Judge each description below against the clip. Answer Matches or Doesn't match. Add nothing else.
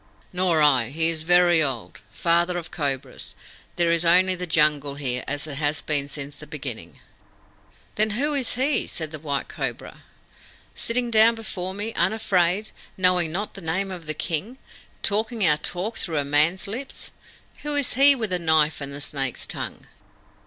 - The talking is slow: Doesn't match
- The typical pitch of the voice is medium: Matches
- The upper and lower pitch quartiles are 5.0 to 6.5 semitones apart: Matches